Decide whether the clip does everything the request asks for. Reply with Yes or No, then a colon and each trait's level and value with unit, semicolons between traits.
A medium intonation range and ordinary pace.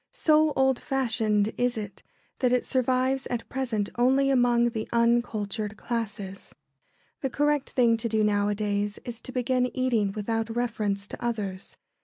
Yes: average, 3.3 semitones; average, 145 wpm